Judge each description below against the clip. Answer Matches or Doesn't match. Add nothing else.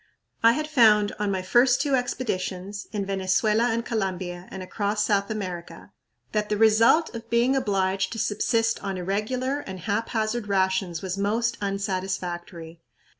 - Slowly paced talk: Doesn't match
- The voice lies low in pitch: Doesn't match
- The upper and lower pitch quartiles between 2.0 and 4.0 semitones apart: Matches